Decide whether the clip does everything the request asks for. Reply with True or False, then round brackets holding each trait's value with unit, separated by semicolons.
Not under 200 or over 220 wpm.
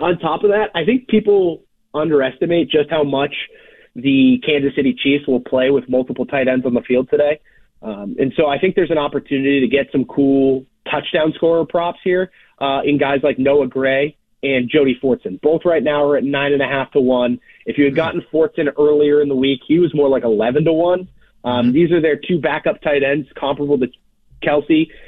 True (205 wpm)